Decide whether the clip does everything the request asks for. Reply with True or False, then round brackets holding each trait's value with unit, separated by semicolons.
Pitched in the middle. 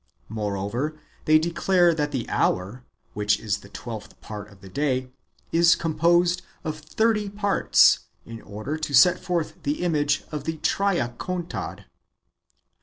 True (150 Hz)